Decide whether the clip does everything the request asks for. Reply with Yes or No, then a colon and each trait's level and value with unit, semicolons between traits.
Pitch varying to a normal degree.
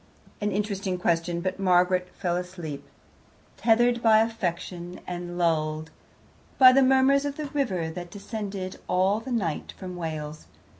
Yes: average, 4.4 semitones